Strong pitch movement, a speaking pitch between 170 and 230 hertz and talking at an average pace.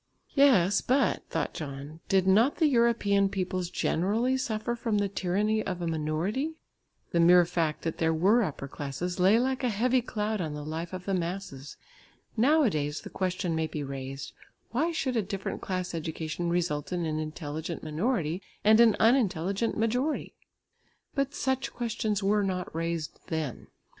Yes: wide, 5.9 semitones; medium, 185 Hz; average, 160 wpm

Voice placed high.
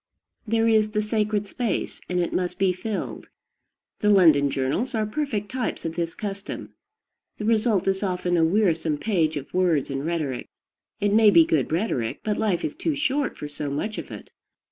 Yes: high, 195 Hz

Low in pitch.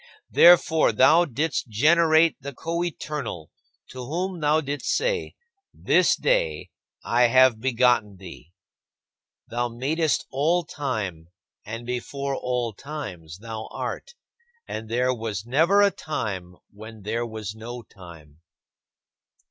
Yes: low, 125 Hz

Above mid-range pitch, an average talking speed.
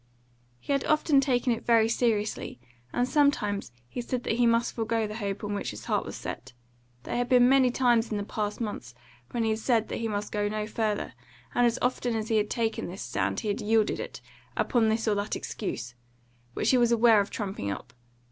No: high, 225 Hz; fast, 220 wpm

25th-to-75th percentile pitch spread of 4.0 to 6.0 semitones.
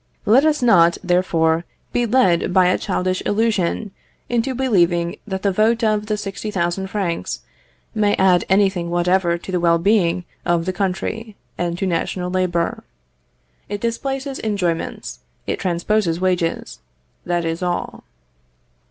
No: average, 3.6 semitones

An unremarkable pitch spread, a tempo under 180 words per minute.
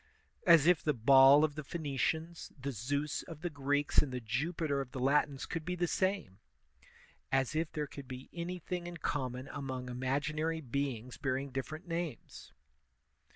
Yes: average, 3.5 semitones; average, 160 wpm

